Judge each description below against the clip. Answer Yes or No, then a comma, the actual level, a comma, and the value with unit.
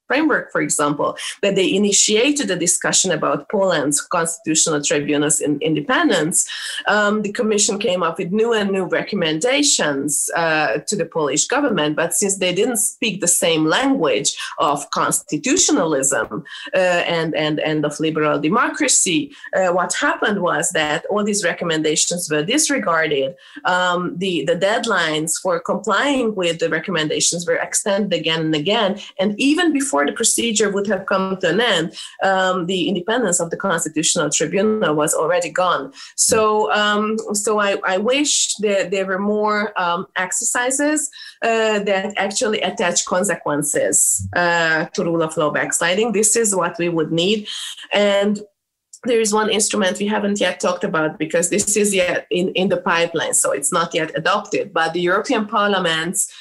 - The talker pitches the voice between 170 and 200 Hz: Yes, high, 190 Hz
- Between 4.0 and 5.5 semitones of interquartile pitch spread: Yes, average, 4.6 semitones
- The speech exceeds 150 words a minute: Yes, average, 160 wpm